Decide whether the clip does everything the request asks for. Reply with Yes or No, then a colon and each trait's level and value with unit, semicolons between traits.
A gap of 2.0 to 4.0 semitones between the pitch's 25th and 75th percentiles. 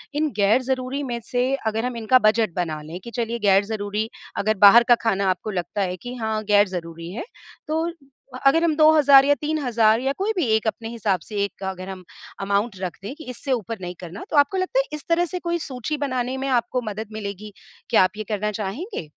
No: average, 5.2 semitones